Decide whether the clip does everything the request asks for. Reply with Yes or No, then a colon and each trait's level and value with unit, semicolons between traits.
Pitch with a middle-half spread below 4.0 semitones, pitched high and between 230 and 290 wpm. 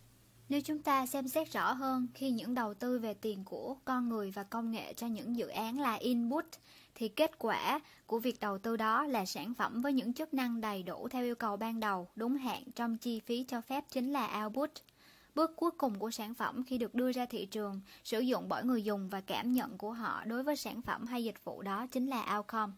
Yes: average, 3.3 semitones; high, 235 Hz; average, 235 wpm